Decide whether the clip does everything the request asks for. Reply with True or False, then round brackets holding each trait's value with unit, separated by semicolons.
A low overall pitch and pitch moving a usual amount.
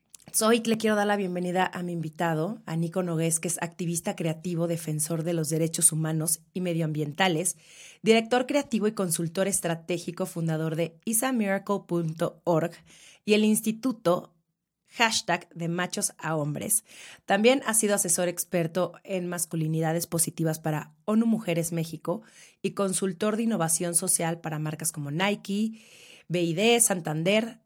False (175 Hz; 3.8 semitones)